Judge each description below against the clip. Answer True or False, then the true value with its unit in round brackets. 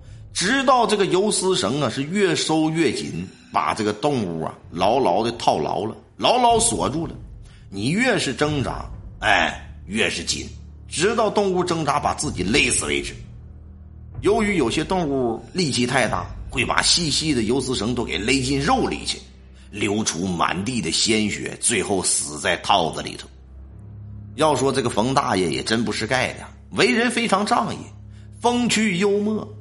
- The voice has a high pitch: False (135 Hz)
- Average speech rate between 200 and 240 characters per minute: True (235 characters per minute)